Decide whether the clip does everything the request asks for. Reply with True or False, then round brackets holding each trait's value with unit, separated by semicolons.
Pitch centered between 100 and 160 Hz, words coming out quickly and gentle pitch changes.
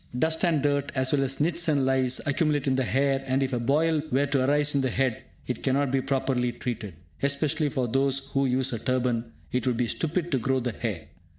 True (135 Hz; 225 wpm; 2.2 semitones)